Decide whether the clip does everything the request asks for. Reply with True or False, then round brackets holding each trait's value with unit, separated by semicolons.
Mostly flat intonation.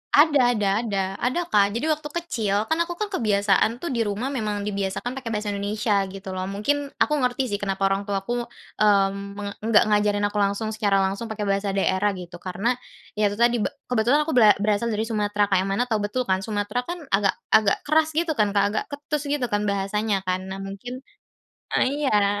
False (3.5 semitones)